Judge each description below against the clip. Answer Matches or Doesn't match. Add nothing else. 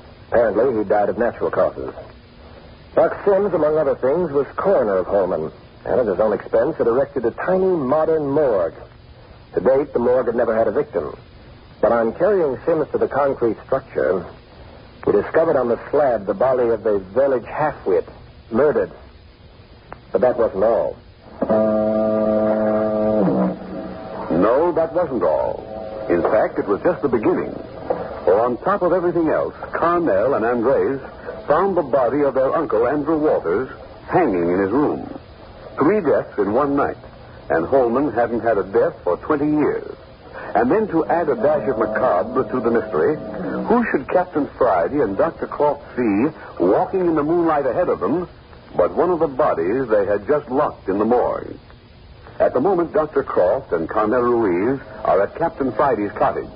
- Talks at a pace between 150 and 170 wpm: Matches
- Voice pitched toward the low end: Doesn't match